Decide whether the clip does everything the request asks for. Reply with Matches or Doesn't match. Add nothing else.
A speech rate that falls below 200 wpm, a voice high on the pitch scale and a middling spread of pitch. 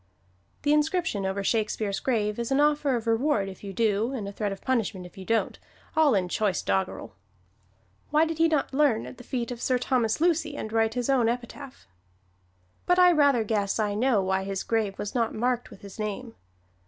Doesn't match